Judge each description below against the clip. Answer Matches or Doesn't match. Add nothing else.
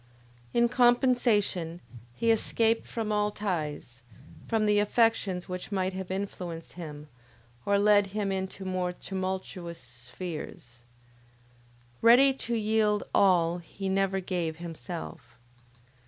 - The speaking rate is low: Matches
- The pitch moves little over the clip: Doesn't match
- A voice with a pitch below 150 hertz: Doesn't match